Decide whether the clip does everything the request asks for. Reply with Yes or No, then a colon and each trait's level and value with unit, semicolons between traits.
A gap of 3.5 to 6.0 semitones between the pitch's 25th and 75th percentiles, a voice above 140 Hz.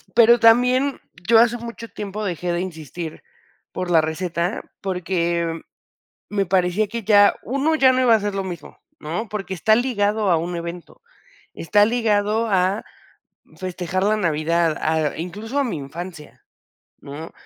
Yes: average, 4.6 semitones; high, 190 Hz